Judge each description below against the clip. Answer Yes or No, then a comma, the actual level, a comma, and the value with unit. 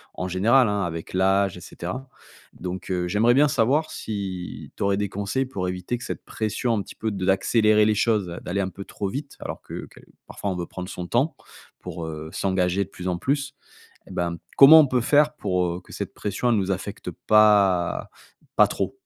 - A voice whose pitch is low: Yes, low, 100 Hz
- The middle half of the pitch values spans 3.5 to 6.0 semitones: Yes, average, 4.3 semitones